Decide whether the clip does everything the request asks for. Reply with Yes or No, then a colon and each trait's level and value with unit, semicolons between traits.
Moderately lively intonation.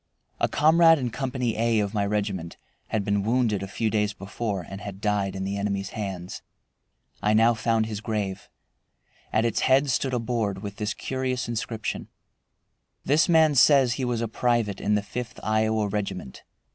Yes: average, 3.3 semitones